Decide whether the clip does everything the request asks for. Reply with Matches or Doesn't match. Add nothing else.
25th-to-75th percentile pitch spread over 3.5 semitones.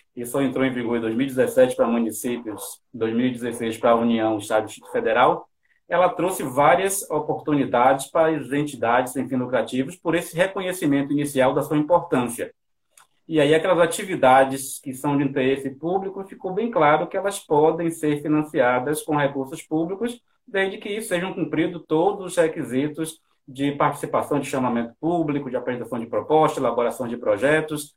Matches